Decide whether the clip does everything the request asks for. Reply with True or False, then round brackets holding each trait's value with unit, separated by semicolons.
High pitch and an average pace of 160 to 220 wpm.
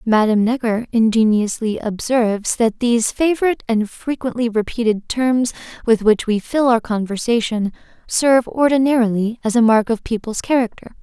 False (230 Hz; 135 wpm)